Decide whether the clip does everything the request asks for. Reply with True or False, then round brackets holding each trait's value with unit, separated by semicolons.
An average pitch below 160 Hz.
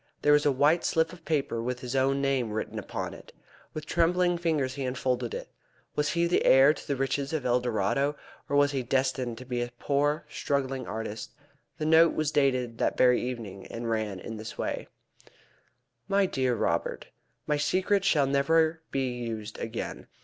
True (135 Hz)